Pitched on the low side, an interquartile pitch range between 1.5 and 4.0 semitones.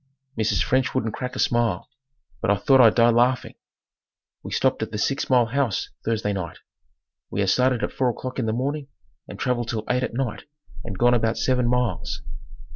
Yes: low, 120 Hz; narrow, 2.6 semitones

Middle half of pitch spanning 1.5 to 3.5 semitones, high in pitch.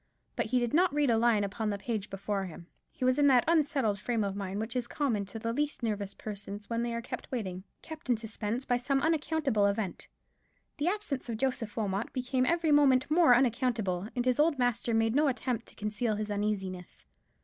No: average, 4.3 semitones; high, 235 Hz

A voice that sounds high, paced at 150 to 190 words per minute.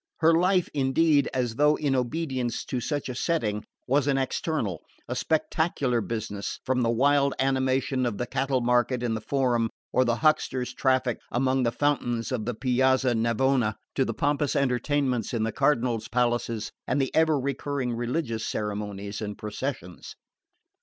No: low, 125 Hz; average, 160 wpm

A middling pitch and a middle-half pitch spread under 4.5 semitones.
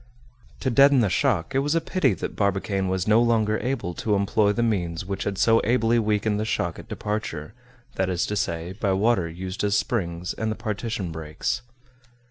No: low, 105 Hz; average, 3.5 semitones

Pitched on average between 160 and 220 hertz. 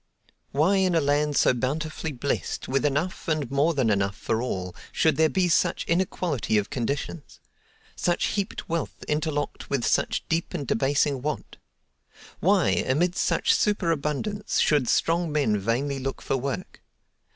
No: medium, 150 Hz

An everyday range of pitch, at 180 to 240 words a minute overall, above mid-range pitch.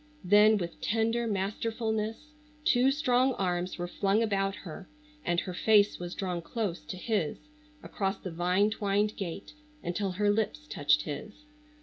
No: average, 3.7 semitones; average, 145 wpm; high, 200 Hz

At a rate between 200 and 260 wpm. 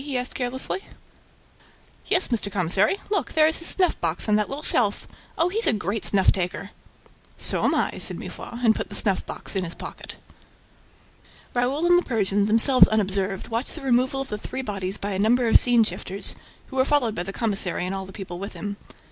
Yes: fast, 205 wpm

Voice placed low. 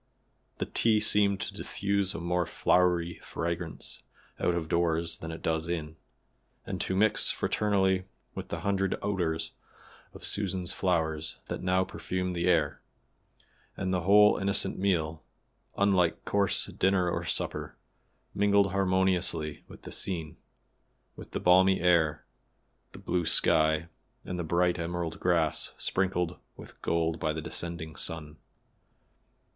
Yes: very low, 90 Hz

